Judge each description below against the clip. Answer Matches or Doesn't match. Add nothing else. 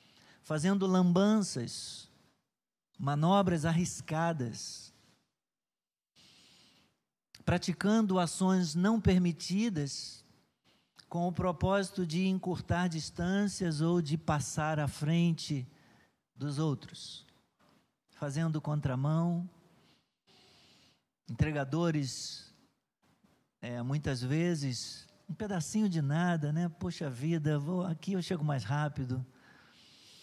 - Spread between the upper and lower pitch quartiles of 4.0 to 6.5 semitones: Doesn't match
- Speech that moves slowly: Matches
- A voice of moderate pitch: Matches